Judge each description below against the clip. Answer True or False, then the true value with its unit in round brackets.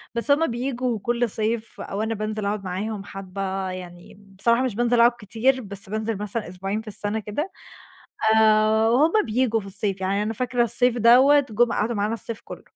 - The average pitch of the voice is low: False (220 Hz)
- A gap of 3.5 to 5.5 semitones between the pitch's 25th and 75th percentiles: False (2.9 semitones)